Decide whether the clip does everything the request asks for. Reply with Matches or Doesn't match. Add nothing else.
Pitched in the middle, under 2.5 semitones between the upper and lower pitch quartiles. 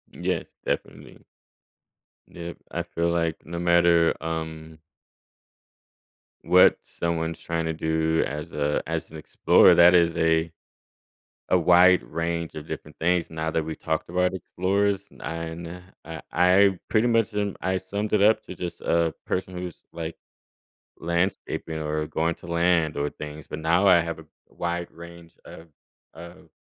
Doesn't match